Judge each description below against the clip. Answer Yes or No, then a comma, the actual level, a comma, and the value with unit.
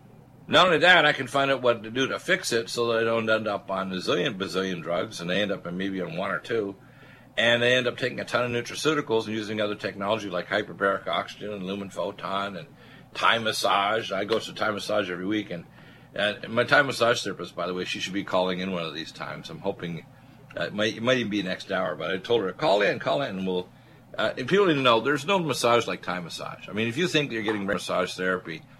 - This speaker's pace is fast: Yes, fast, 260 wpm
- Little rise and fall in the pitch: No, average, 4.2 semitones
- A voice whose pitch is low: Yes, low, 105 Hz